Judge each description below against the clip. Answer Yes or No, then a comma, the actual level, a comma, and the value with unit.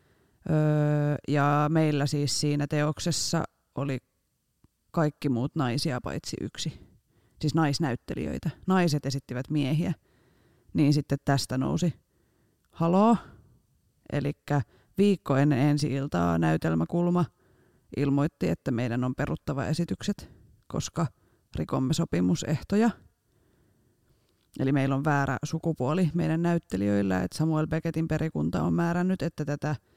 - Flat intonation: No, average, 4.5 semitones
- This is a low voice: No, medium, 145 Hz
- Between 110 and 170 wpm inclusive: No, average, 100 wpm